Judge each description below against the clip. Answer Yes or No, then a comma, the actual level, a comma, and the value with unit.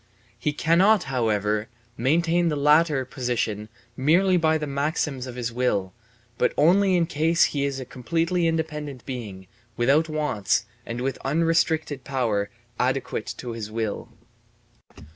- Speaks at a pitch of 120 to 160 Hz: Yes, medium, 140 Hz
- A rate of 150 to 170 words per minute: No, slow, 135 wpm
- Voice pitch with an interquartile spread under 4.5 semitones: No, average, 5.2 semitones